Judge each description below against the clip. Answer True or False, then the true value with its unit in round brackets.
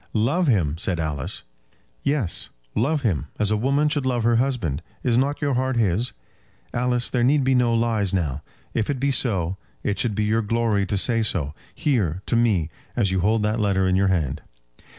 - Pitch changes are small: False (4.9 semitones)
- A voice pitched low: True (110 Hz)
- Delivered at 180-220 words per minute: True (195 wpm)